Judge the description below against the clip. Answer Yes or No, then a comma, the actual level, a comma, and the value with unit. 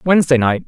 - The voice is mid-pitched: Yes, medium, 145 Hz